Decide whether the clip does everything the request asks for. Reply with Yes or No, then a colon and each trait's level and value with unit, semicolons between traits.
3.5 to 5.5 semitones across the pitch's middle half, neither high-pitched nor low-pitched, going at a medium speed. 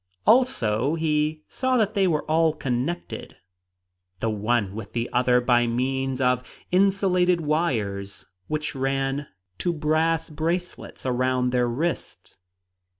No: average, 5.1 semitones; medium, 145 Hz; slow, 120 wpm